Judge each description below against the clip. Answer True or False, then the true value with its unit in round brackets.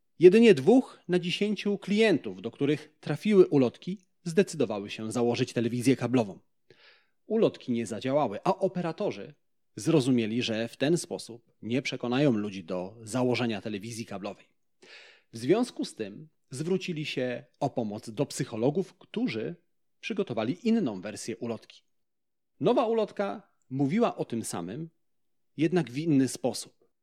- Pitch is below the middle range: False (145 Hz)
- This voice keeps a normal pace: True (125 wpm)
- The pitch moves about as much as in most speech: False (7.5 semitones)